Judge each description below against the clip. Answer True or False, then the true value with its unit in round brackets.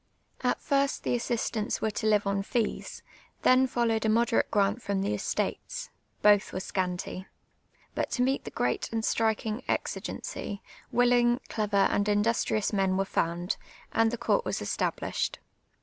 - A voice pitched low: False (220 Hz)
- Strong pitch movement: False (3.2 semitones)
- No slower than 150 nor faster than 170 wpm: True (155 wpm)